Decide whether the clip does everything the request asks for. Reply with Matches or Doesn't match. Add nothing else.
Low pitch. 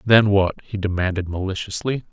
Matches